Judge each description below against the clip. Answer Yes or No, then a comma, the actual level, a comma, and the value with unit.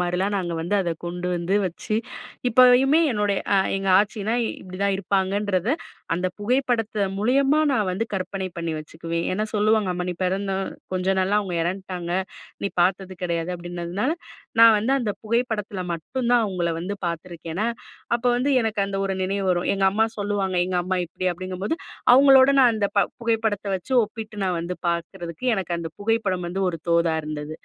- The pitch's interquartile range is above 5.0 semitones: No, average, 3.5 semitones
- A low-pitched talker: No, high, 195 Hz